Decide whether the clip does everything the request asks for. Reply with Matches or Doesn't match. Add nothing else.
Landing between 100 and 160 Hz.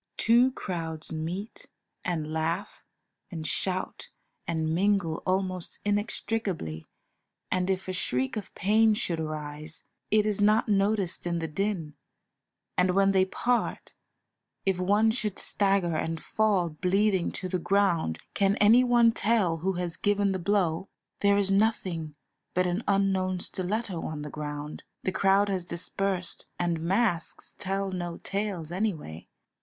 Doesn't match